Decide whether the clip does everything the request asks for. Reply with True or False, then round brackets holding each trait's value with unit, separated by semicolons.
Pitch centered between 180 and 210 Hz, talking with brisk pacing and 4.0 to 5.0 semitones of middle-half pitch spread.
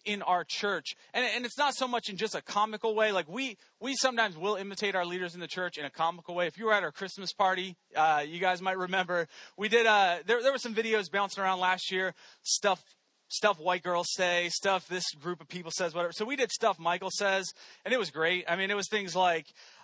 False (190 Hz; 240 wpm; 3.3 semitones)